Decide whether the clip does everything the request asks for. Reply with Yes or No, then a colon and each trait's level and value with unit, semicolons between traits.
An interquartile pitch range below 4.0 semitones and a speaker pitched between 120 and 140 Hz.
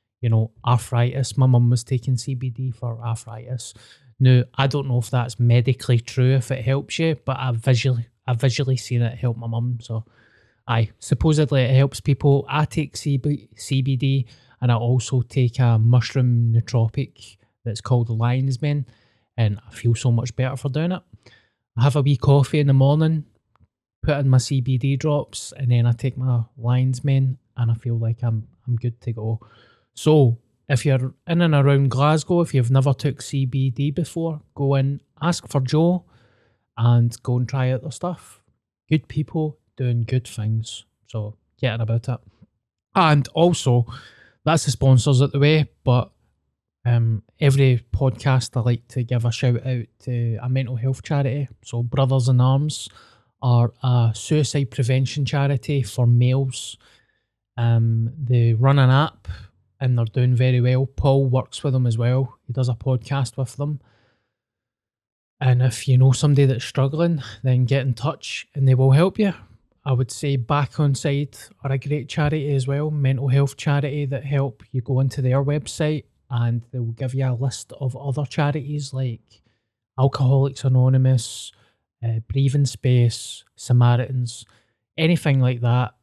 Yes: average, 2.8 semitones; low, 130 Hz